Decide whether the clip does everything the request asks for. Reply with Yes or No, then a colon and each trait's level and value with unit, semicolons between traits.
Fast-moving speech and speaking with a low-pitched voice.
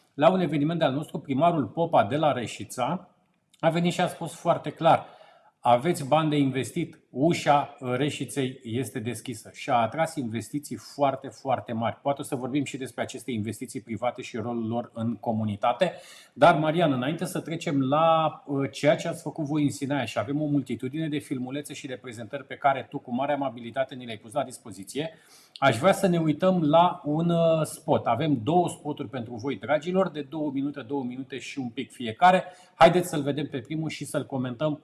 No: fast, 190 wpm; medium, 145 Hz